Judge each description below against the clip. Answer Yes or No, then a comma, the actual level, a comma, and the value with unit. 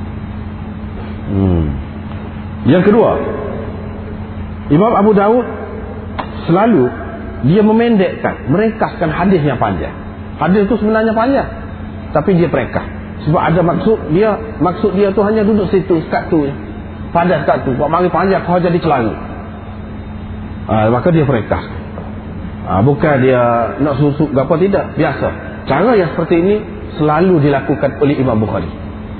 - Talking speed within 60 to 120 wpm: No, average, 130 wpm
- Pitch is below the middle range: Yes, low, 130 Hz